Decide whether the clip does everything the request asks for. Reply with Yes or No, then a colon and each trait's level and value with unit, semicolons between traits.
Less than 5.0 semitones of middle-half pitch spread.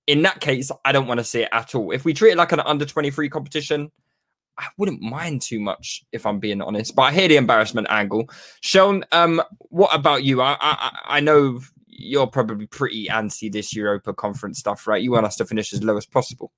No: wide, 5.5 semitones